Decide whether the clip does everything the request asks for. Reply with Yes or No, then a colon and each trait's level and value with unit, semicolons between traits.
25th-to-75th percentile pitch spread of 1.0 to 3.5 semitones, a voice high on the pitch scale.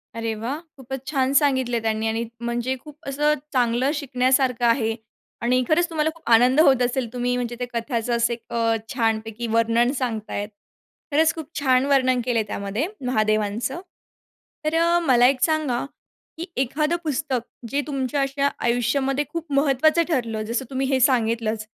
Yes: average, 3.2 semitones; very high, 255 Hz